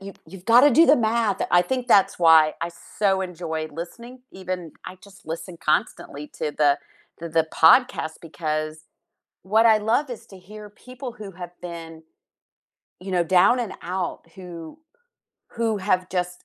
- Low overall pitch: No, medium, 185 Hz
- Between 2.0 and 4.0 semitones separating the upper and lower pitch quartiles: No, average, 4.8 semitones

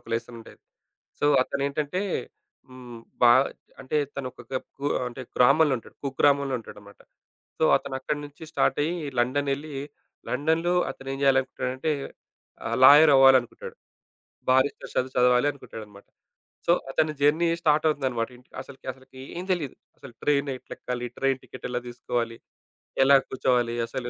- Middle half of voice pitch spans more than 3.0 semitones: No, average, 2.7 semitones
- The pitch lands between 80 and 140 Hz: Yes, low, 135 Hz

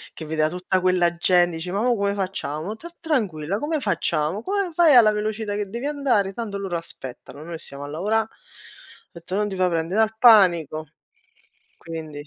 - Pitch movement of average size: Yes, average, 4.9 semitones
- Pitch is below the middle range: No, high, 190 Hz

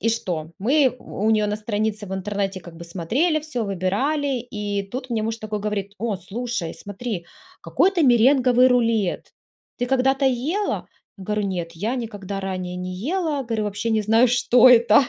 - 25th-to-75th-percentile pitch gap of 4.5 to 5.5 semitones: No, average, 4.0 semitones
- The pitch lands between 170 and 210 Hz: No, high, 220 Hz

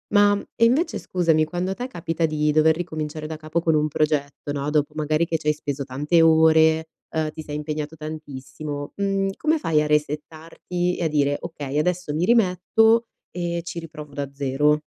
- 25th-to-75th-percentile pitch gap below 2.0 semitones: No, narrow, 2.4 semitones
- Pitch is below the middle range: No, medium, 155 Hz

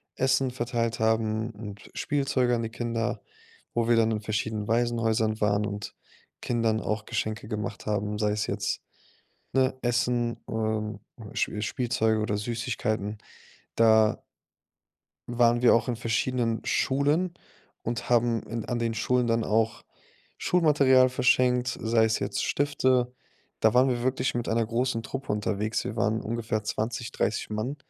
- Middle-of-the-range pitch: No, low, 115 Hz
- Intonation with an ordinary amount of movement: No, narrow, 2.1 semitones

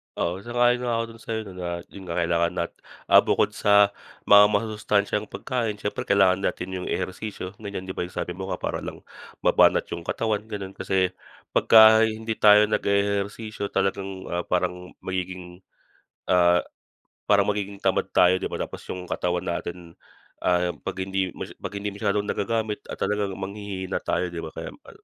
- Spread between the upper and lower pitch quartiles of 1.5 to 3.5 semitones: Yes, narrow, 2.4 semitones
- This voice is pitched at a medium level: No, low, 100 Hz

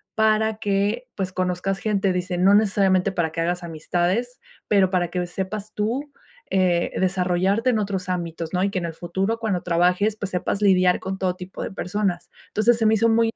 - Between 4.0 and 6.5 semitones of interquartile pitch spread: No, average, 2.8 semitones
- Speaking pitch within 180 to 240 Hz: Yes, high, 190 Hz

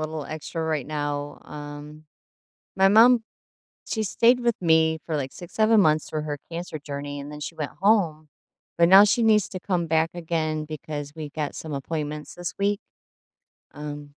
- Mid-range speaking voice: Yes, medium, 155 Hz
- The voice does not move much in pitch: No, average, 3.4 semitones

